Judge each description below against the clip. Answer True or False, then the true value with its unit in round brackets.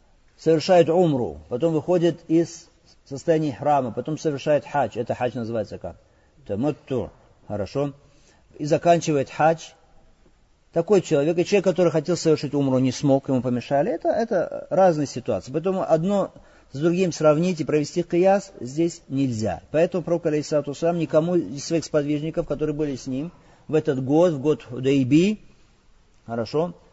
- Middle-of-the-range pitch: True (155 Hz)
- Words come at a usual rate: True (145 wpm)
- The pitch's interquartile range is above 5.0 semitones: False (3.7 semitones)